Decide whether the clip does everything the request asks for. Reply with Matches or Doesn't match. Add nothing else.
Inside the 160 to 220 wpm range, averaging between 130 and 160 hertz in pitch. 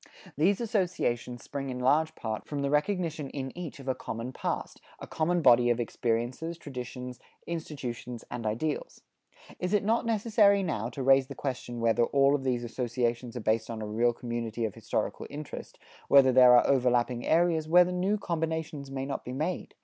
Matches